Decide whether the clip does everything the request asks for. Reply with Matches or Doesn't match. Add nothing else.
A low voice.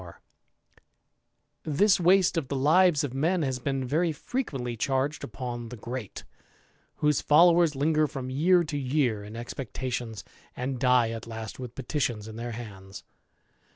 Matches